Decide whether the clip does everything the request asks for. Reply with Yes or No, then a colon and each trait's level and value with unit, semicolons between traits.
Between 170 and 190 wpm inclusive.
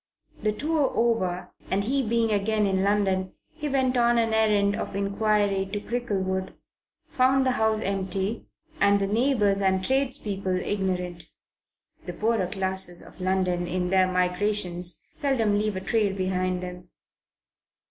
No: average, 140 wpm